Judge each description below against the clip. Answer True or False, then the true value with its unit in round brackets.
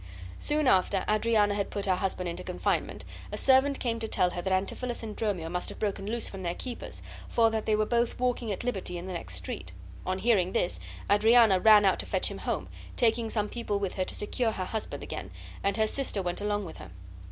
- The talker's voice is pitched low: False (205 Hz)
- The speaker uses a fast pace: True (225 wpm)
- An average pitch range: True (3.5 semitones)